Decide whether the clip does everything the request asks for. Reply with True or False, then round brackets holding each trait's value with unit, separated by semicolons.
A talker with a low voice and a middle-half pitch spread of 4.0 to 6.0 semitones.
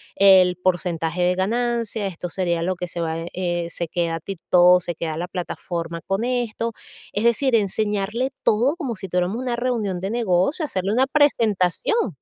False (190 Hz; 4.7 semitones)